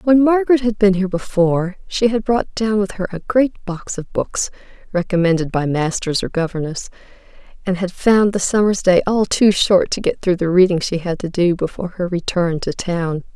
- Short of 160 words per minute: No, average, 200 wpm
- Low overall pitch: No, high, 190 Hz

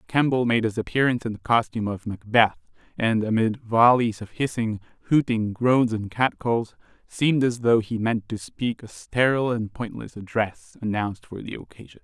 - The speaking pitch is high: No, low, 115 Hz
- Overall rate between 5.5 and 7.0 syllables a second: No, 5.0 syllables/s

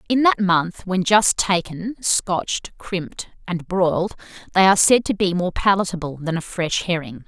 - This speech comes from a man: No, female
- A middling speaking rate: Yes, average, 175 wpm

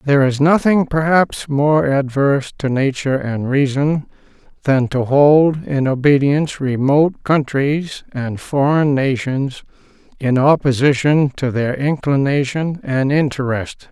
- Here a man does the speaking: Yes, male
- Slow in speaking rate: Yes, slow, 115 wpm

